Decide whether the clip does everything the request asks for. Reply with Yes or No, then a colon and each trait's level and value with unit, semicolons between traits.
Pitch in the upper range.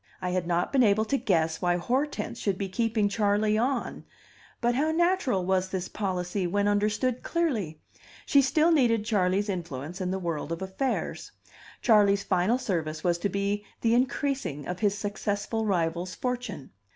Yes: high, 205 Hz